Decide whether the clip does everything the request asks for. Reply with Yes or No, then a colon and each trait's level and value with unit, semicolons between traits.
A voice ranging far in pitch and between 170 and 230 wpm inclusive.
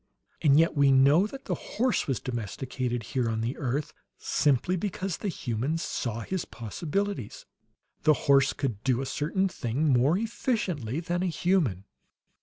No: wide, 6.5 semitones; average, 155 wpm